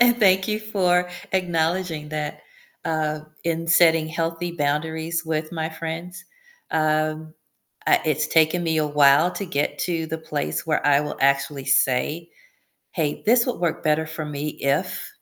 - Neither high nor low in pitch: Yes, medium, 160 Hz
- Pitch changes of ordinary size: No, narrow, 2.3 semitones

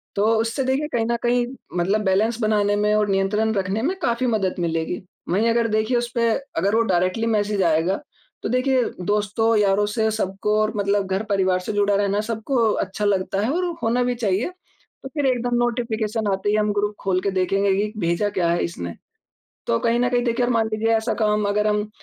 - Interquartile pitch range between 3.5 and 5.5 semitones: No, average, 2.9 semitones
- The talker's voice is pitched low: No, high, 210 Hz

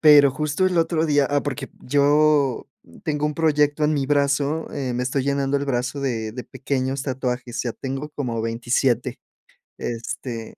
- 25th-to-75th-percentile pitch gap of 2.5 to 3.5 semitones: Yes, average, 2.8 semitones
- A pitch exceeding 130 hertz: Yes, medium, 140 Hz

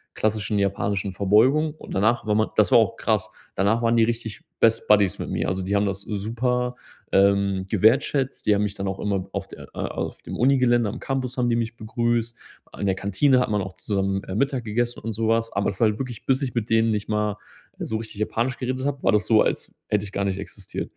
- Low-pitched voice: Yes, low, 110 Hz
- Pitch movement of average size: Yes, average, 3.1 semitones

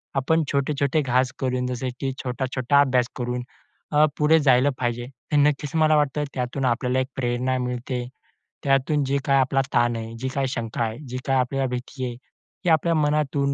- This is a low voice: Yes, low, 130 Hz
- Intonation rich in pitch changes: No, narrow, 2.4 semitones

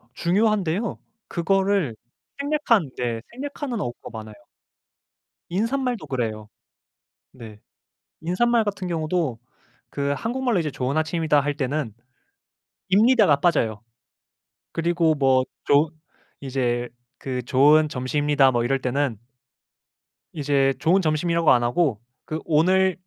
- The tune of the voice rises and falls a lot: Yes, wide, 6.4 semitones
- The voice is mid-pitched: Yes, medium, 155 Hz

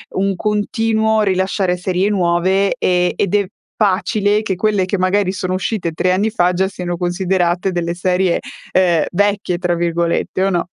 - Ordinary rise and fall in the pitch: No, narrow, 2.3 semitones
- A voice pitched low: No, medium, 185 Hz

